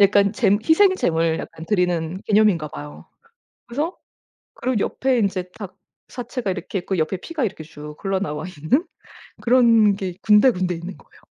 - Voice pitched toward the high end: Yes, high, 195 Hz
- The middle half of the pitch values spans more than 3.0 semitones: Yes, average, 5.1 semitones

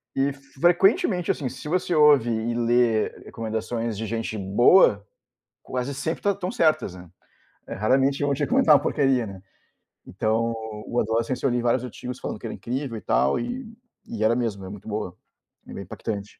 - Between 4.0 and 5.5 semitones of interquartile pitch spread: Yes, average, 4.3 semitones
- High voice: No, low, 120 Hz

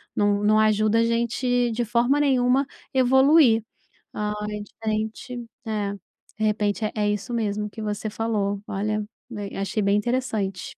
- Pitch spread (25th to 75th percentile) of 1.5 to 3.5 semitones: Yes, narrow, 2.6 semitones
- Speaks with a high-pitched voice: Yes, high, 215 Hz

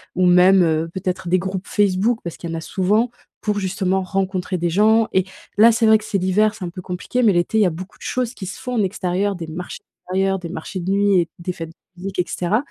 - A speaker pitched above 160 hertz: Yes, high, 190 Hz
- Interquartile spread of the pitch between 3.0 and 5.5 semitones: No, narrow, 2.5 semitones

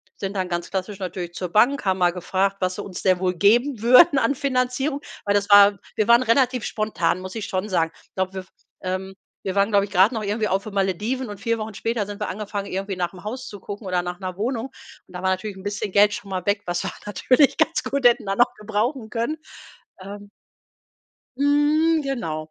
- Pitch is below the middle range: No, high, 205 Hz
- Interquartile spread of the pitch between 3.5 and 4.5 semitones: Yes, average, 4.0 semitones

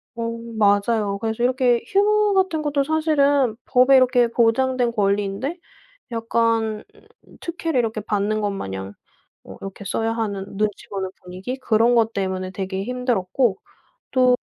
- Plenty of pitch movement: No, average, 4.2 semitones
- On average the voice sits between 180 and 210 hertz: No, high, 230 Hz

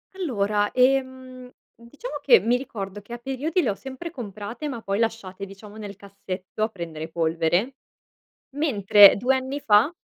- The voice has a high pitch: Yes, high, 225 Hz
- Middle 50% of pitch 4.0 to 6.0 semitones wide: Yes, average, 4.7 semitones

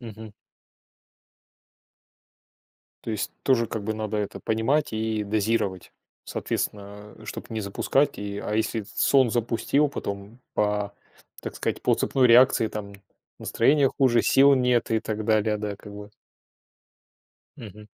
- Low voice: Yes, low, 110 Hz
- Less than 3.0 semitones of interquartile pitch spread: Yes, narrow, 2.5 semitones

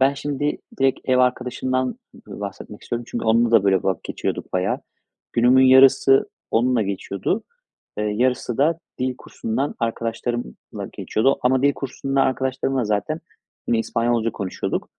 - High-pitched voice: No, low, 125 Hz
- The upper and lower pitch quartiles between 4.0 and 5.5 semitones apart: No, average, 3.0 semitones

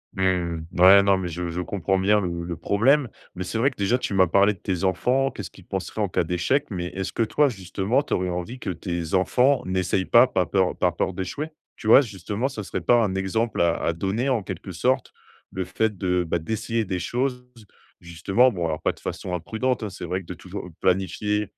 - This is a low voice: Yes, very low, 95 Hz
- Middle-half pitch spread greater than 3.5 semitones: Yes, average, 4.0 semitones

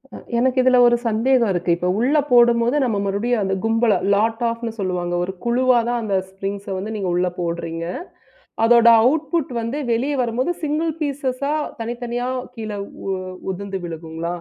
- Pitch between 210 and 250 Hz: Yes, high, 230 Hz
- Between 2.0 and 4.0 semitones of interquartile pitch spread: No, average, 4.4 semitones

